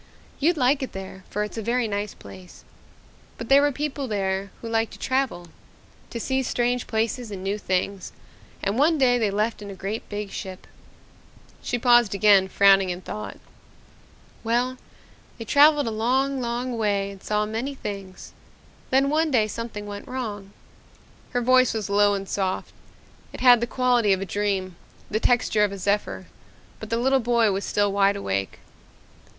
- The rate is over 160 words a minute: Yes, average, 175 wpm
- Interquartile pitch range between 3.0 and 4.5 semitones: Yes, average, 3.9 semitones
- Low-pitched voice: No, high, 215 Hz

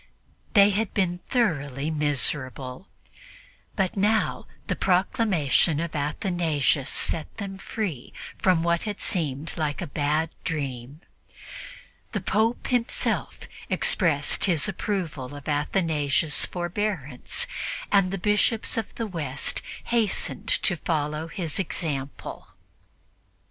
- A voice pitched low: No, medium, 170 Hz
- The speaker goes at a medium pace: No, slow, 105 wpm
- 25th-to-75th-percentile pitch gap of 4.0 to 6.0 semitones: Yes, average, 5.2 semitones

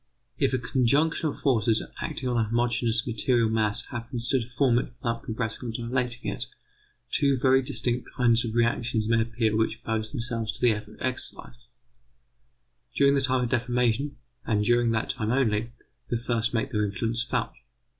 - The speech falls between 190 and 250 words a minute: No, average, 170 wpm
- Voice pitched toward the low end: Yes, low, 120 Hz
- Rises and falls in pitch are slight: Yes, narrow, 2.0 semitones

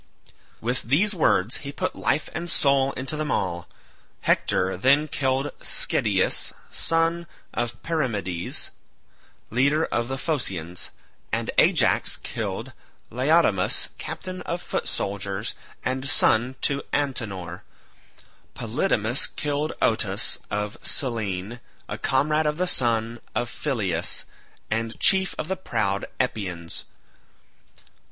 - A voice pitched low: Yes, low, 125 Hz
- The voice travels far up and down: Yes, wide, 6.6 semitones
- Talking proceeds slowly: Yes, slow, 110 wpm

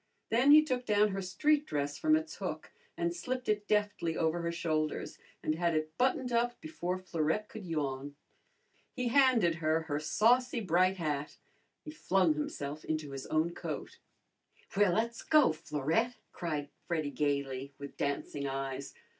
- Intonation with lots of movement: Yes, wide, 7.5 semitones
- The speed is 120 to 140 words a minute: No, average, 155 wpm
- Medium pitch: Yes, medium, 170 Hz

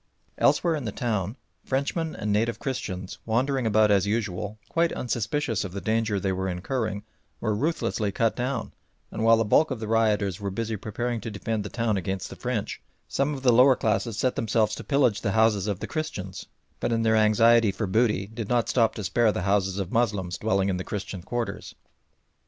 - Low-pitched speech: Yes, low, 110 Hz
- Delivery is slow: No, average, 200 wpm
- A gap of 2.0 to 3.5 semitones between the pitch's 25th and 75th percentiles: Yes, average, 2.9 semitones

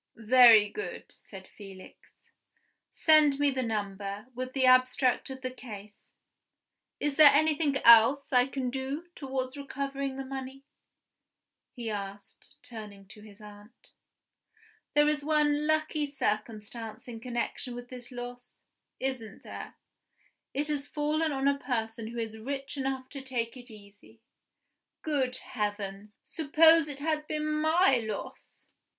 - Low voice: No, very high, 255 Hz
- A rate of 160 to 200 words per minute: No, slow, 135 wpm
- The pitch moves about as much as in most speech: Yes, average, 4.3 semitones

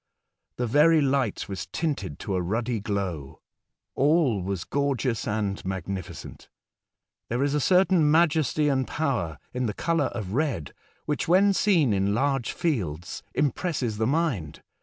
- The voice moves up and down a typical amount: No, wide, 7.3 semitones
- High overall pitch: No, low, 125 Hz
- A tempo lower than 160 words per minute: Yes, average, 140 wpm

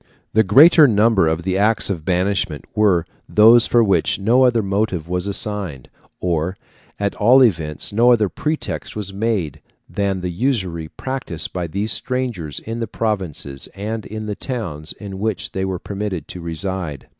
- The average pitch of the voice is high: No, low, 100 Hz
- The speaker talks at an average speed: Yes, average, 165 wpm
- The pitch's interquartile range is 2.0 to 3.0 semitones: No, average, 4.2 semitones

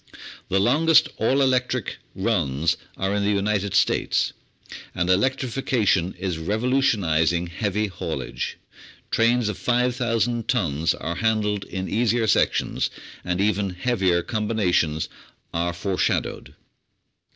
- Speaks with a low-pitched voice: Yes, low, 105 Hz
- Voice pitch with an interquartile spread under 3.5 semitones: No, average, 4.9 semitones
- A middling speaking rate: No, slow, 110 wpm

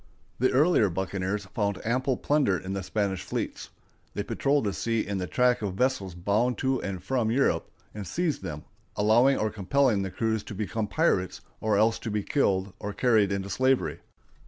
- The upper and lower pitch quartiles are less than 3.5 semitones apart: No, average, 4.5 semitones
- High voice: No, low, 105 Hz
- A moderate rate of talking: Yes, average, 180 wpm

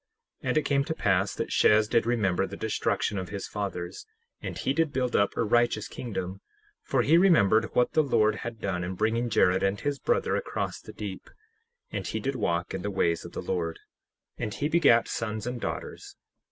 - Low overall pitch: Yes, low, 110 Hz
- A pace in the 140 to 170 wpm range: No, fast, 205 wpm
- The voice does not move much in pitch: No, average, 4.3 semitones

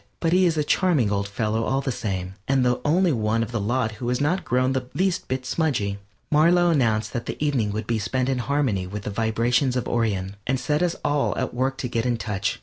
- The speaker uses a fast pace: Yes, fast, 240 wpm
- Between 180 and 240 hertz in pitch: No, low, 125 Hz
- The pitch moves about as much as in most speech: Yes, average, 5.0 semitones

